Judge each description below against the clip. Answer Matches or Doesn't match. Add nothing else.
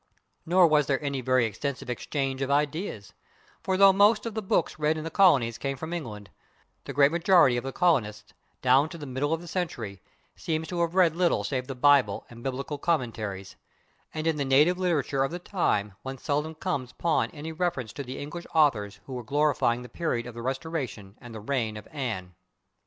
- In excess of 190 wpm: Matches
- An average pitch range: Matches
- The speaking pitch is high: Doesn't match